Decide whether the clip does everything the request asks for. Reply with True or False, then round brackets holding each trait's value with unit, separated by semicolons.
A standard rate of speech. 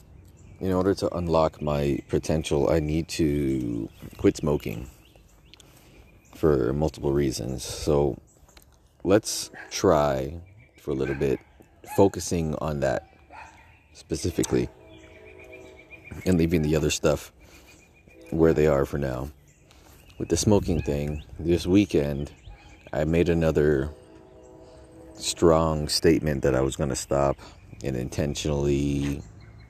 False (110 wpm)